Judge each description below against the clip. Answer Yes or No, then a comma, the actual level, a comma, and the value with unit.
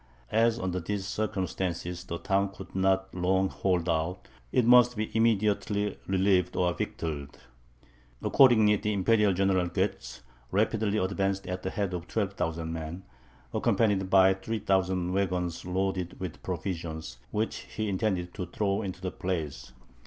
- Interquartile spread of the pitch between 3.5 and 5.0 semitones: No, narrow, 2.4 semitones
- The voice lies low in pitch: Yes, very low, 95 Hz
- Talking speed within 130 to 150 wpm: Yes, average, 140 wpm